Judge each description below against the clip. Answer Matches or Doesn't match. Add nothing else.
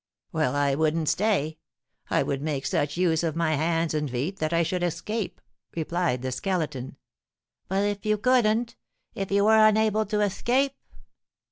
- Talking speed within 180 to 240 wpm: Doesn't match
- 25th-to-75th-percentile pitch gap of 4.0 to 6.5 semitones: Matches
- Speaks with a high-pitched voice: Doesn't match